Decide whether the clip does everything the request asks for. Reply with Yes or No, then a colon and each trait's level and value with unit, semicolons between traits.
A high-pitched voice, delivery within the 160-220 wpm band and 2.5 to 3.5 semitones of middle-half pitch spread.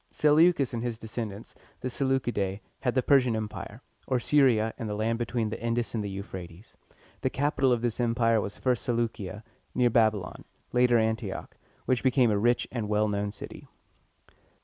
No: low, 115 Hz; average, 190 wpm; average, 2.8 semitones